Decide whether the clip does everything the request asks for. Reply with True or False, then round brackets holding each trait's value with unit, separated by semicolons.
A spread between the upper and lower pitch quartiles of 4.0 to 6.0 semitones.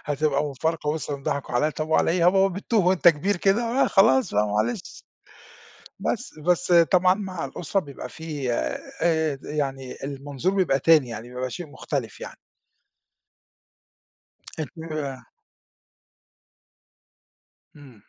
True (4.6 semitones)